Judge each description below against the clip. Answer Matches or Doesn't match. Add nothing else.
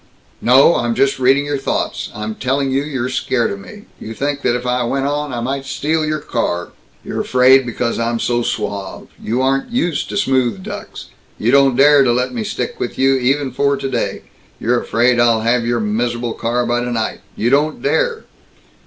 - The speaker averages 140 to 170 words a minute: Doesn't match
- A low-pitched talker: Matches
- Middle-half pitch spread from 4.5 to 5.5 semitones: Doesn't match